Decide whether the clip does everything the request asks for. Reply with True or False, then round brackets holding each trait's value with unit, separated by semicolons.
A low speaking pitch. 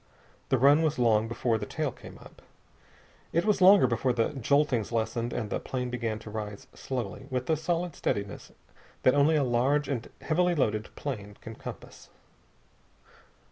True (125 Hz)